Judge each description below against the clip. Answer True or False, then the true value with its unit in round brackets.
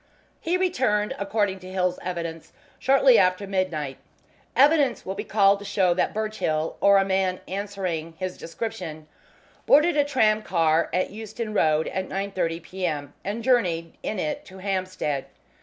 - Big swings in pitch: False (3.9 semitones)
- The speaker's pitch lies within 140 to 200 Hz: True (190 Hz)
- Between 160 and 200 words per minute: False (145 wpm)